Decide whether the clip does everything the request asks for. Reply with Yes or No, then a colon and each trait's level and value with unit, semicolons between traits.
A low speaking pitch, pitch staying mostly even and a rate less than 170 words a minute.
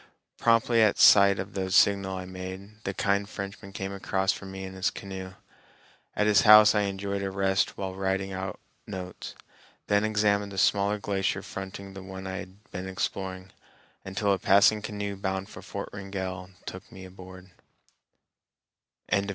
Yes: very low, 95 Hz; narrow, 1.1 semitones; average, 160 wpm